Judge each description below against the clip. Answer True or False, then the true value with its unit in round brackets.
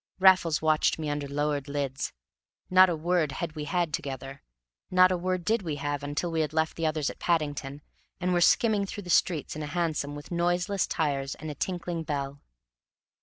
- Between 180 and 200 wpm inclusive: True (195 wpm)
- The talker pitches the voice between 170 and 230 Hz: False (155 Hz)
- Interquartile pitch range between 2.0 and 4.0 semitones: True (3.4 semitones)